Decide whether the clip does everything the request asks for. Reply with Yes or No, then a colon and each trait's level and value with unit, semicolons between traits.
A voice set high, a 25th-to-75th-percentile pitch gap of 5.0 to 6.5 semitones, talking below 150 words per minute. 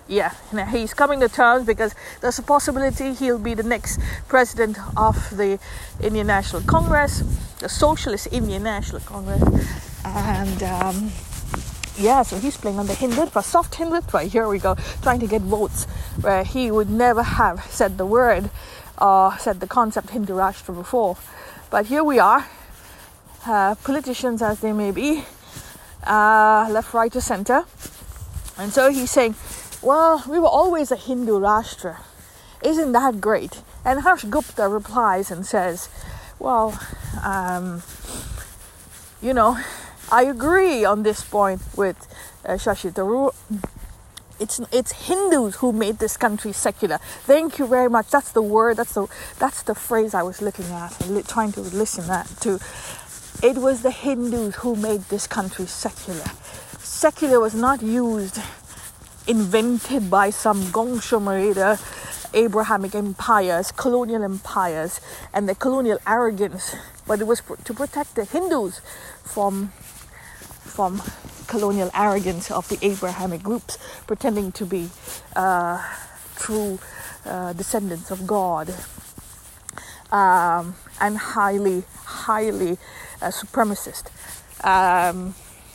No: high, 215 Hz; average, 3.9 semitones; slow, 135 wpm